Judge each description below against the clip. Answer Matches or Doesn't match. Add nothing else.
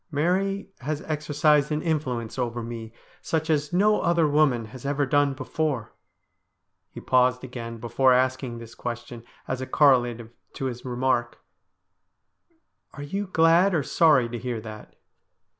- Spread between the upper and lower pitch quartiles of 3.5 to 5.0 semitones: Matches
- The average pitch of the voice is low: Matches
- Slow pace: Doesn't match